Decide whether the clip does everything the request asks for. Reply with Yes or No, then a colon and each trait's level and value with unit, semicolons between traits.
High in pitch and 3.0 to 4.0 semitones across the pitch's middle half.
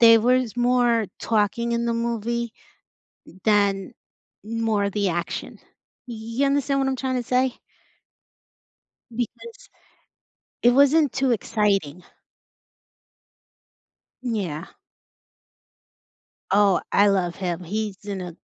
Yes: high, 230 Hz; average, 3.7 semitones